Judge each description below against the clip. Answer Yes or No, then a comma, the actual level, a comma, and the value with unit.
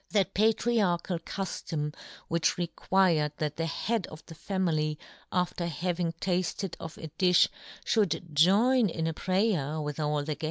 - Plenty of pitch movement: No, average, 3.4 semitones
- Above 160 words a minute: No, average, 155 wpm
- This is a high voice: No, medium, 170 Hz